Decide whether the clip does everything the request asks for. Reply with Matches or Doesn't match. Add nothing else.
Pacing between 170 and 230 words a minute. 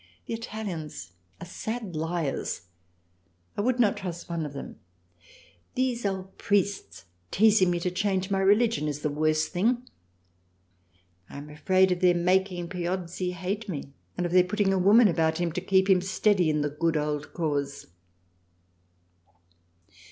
Doesn't match